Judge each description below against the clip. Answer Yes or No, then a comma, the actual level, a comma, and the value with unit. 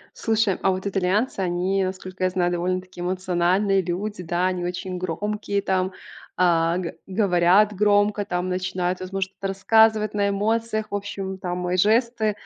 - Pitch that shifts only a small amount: Yes, narrow, 2.2 semitones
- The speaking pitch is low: No, high, 190 Hz